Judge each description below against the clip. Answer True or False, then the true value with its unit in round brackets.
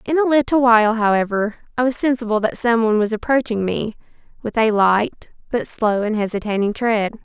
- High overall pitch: True (225 Hz)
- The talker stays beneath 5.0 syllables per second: False (5.4 syllables/s)